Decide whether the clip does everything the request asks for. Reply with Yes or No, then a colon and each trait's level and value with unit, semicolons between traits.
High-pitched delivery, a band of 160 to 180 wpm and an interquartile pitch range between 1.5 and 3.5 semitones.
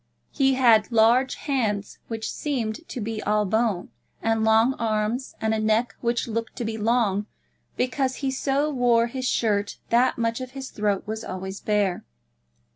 Yes: high, 230 Hz; average, 165 wpm; average, 2.9 semitones